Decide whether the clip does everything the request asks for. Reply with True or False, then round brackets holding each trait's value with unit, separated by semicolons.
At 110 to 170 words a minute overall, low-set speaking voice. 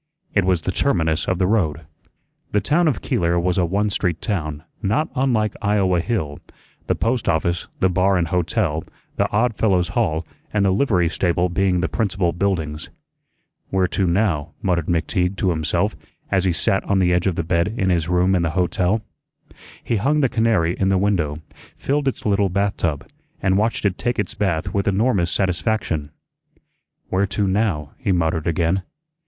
False (180 wpm; 95 Hz)